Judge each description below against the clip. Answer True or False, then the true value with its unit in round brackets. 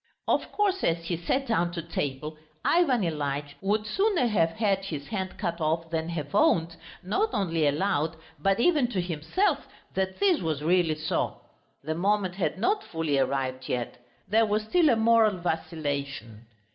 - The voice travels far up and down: True (5.9 semitones)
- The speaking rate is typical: True (165 wpm)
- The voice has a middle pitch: True (175 Hz)